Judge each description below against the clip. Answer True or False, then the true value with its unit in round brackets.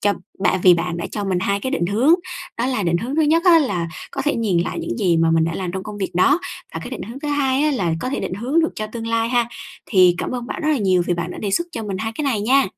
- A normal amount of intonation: False (6.6 semitones)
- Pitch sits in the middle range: False (215 Hz)